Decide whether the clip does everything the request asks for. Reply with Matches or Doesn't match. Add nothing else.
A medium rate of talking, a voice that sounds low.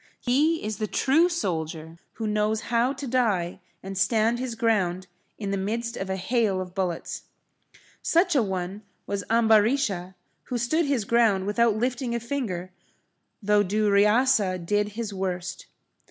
Doesn't match